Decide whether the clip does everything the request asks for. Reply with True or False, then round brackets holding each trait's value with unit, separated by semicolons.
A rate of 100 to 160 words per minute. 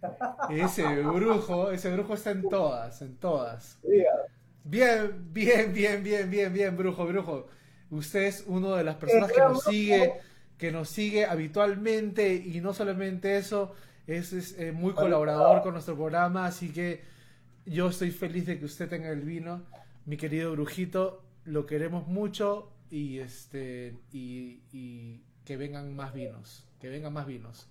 True (150 wpm)